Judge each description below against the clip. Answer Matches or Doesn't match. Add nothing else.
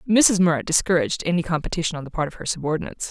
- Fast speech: Matches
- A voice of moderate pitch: Matches